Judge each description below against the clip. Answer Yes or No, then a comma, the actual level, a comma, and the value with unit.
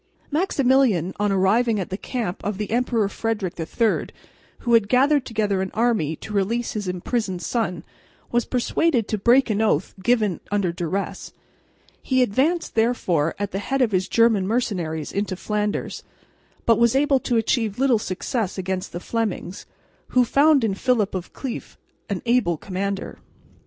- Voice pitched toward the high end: Yes, high, 215 Hz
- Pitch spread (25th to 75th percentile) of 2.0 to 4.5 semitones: Yes, average, 4.2 semitones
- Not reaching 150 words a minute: No, average, 155 wpm